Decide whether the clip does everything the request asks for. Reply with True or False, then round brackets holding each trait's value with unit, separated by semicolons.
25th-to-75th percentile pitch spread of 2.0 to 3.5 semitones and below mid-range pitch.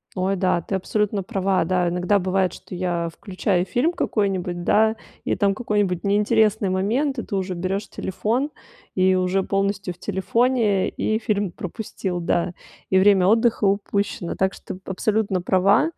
False (2.4 semitones; 195 Hz)